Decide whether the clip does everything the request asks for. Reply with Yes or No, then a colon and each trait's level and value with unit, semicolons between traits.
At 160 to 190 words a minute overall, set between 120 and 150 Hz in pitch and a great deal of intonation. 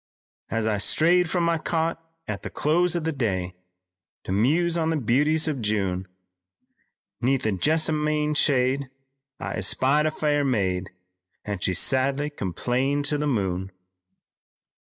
No: average, 140 wpm; medium, 140 Hz; wide, 6.4 semitones